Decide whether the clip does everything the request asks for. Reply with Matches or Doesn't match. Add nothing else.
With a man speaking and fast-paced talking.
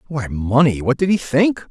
Matches